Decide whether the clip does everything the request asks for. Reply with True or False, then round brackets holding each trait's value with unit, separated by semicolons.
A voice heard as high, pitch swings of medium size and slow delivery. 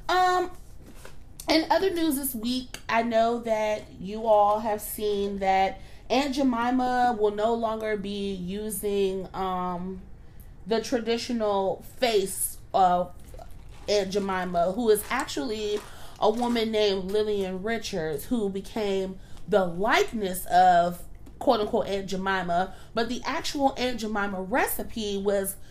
True (215 Hz; 3.6 semitones; 120 wpm)